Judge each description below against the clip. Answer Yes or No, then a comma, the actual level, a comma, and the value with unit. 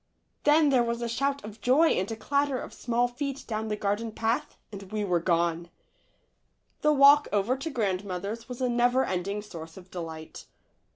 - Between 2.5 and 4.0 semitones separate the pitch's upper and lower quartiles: No, average, 5.2 semitones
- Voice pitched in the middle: No, high, 225 Hz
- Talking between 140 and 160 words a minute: No, fast, 205 wpm